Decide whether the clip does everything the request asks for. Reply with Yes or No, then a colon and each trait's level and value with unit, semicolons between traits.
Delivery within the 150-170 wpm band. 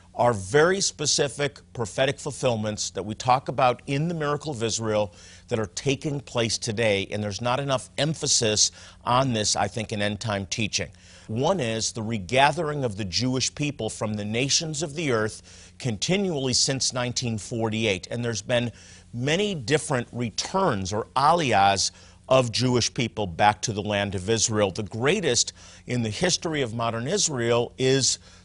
Yes: average, 160 wpm